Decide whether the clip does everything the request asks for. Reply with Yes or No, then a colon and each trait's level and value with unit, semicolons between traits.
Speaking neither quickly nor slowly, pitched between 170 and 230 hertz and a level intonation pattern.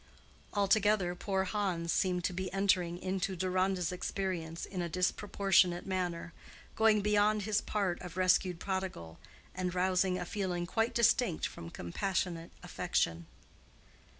No: slow, 125 wpm; medium, 185 Hz; narrow, 2.0 semitones